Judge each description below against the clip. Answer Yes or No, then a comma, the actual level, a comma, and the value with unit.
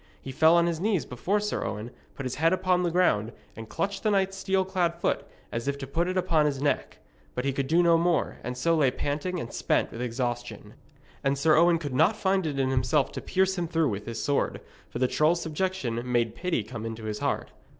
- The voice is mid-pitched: Yes, medium, 150 Hz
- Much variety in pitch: Yes, wide, 6.1 semitones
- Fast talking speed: Yes, fast, 235 wpm